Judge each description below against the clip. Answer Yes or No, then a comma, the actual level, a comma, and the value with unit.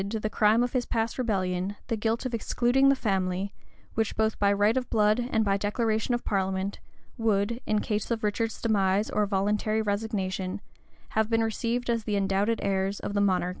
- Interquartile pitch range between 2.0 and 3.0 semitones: Yes, narrow, 2.4 semitones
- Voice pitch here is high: Yes, high, 215 Hz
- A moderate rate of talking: Yes, average, 195 wpm